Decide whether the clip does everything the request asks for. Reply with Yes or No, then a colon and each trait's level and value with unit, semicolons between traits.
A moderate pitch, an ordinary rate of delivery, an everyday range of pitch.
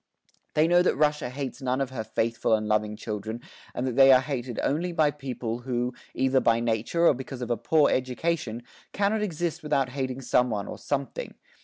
No: low, 130 Hz; average, 195 wpm; average, 4.0 semitones